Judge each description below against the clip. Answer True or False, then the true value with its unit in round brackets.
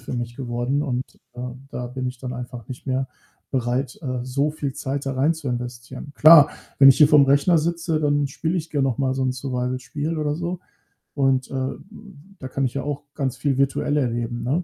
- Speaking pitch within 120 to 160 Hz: True (135 Hz)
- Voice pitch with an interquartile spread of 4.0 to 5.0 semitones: False (2.5 semitones)